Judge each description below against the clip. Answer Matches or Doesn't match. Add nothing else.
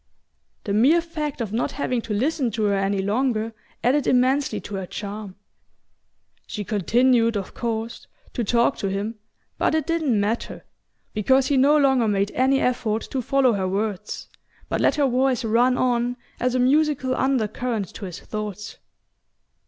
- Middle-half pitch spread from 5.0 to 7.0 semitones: Doesn't match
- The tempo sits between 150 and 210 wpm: Matches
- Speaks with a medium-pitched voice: Doesn't match